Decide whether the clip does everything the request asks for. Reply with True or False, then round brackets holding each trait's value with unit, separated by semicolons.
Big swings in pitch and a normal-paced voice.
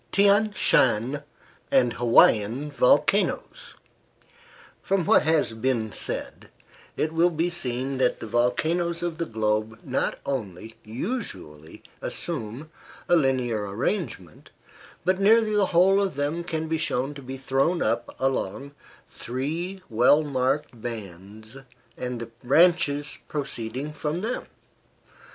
False (6.3 semitones; 120 wpm)